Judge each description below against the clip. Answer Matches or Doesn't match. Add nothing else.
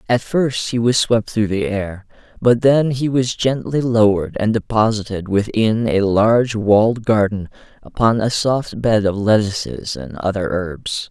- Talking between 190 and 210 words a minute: Doesn't match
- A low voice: Matches